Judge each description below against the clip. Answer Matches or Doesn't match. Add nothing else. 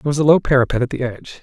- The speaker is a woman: Doesn't match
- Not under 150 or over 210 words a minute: Doesn't match